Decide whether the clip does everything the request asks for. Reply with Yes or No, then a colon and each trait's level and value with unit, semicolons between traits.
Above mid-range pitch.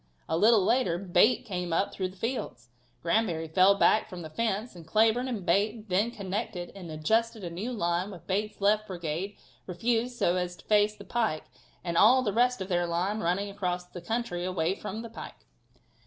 Yes: high, 195 Hz